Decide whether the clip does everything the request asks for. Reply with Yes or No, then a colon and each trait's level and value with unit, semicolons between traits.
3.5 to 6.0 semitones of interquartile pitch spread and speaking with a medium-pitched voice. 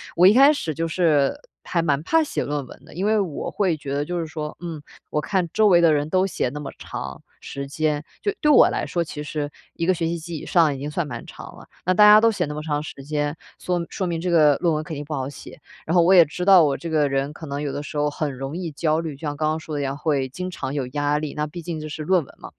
No: average, 3.0 semitones; medium, 155 Hz